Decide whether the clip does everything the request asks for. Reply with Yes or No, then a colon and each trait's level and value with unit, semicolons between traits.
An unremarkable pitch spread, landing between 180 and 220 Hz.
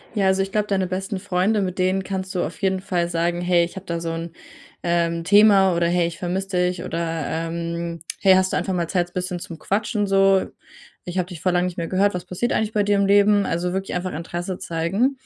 No: narrow, 2.2 semitones; medium, 185 Hz